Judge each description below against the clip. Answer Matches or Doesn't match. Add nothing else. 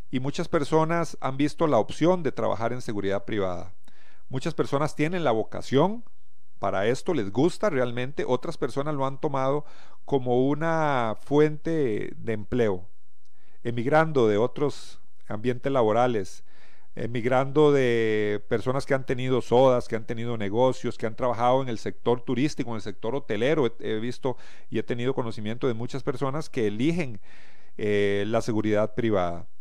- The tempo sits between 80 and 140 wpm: Doesn't match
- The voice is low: Matches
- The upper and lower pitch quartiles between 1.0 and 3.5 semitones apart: Doesn't match